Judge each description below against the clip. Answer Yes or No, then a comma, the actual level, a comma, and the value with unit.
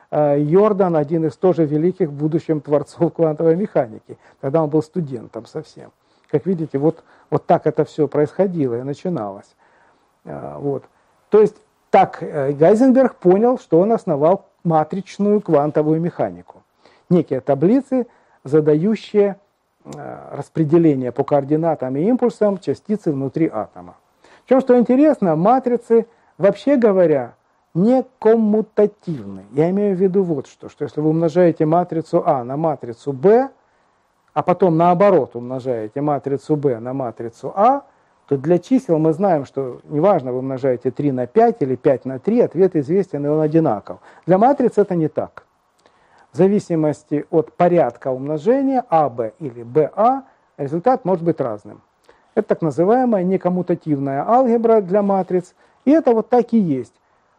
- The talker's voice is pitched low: No, medium, 165 Hz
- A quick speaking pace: No, average, 135 wpm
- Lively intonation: Yes, wide, 5.8 semitones